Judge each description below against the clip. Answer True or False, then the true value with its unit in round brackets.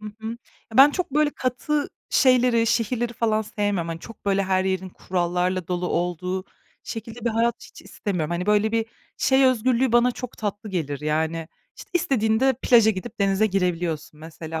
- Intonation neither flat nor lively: True (4.9 semitones)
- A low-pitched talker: False (210 Hz)